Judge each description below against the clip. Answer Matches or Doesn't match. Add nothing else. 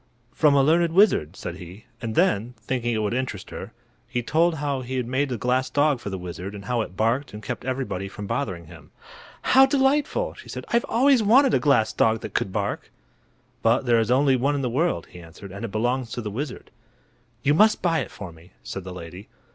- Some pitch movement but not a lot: Doesn't match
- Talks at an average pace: Doesn't match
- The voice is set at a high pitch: Doesn't match